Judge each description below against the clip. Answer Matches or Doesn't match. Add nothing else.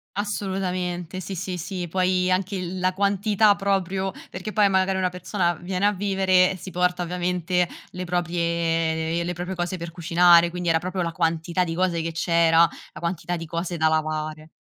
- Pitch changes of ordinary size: Doesn't match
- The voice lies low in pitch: Doesn't match